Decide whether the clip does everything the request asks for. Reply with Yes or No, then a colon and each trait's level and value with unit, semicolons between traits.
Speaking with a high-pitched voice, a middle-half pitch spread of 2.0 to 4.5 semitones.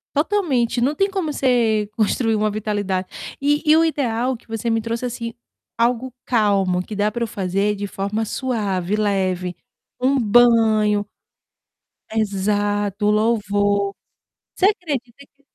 Yes: high, 220 Hz; average, 3.3 semitones